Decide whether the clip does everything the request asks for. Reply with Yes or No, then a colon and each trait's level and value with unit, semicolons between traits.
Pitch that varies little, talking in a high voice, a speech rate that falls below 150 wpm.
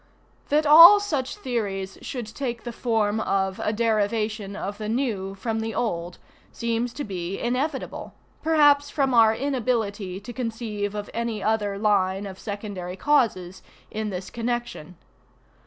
No: average, 3.5 semitones; high, 220 Hz; average, 140 wpm